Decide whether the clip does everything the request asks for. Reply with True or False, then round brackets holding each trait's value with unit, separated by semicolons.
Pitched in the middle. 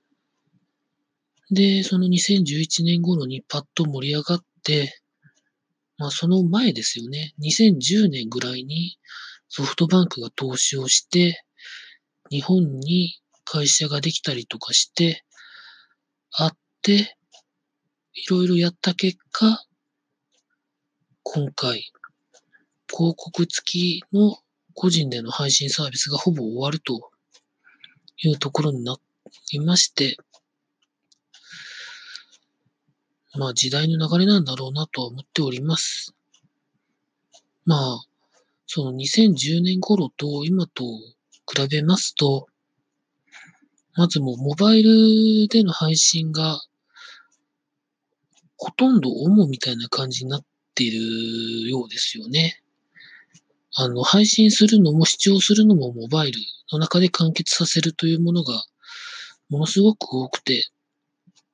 True (160 Hz)